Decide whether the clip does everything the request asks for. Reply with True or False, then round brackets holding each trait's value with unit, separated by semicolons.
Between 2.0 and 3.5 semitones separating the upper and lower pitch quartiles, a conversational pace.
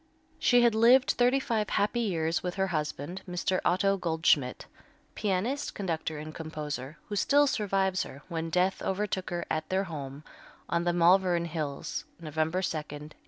False (3.9 semitones; 160 wpm)